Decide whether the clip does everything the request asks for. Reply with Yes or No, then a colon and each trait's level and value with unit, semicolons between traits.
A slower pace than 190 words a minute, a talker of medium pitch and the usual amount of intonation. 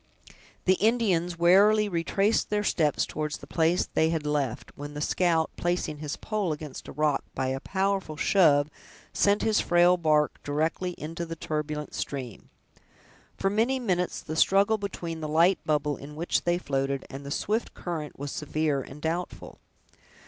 Yes: average, 165 wpm; medium, 165 Hz; average, 3.8 semitones